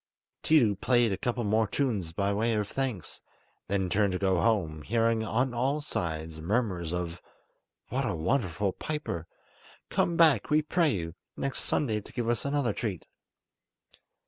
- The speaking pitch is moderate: No, low, 110 Hz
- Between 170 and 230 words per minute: No, average, 155 wpm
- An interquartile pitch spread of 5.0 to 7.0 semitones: Yes, wide, 5.5 semitones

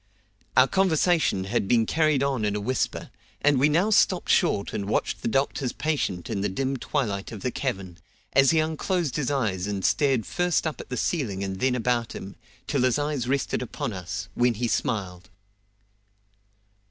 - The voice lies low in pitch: Yes, low, 125 Hz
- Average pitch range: No, wide, 6.1 semitones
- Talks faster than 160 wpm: Yes, average, 180 wpm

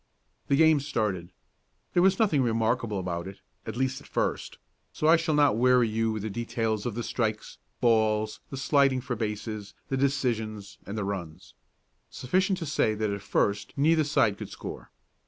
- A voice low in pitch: Yes, low, 115 Hz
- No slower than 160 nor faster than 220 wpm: Yes, average, 175 wpm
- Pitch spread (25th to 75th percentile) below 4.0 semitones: No, average, 4.6 semitones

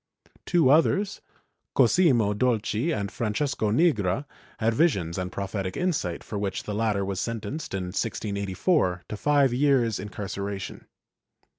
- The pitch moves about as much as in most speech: No, wide, 6.0 semitones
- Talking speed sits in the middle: No, slow, 125 wpm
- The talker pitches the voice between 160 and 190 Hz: No, low, 105 Hz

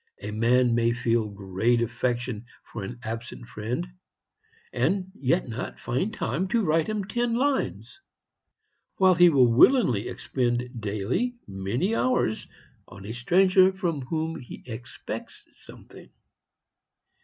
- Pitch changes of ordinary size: No, wide, 8.2 semitones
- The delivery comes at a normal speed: No, slow, 125 wpm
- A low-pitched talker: Yes, low, 125 Hz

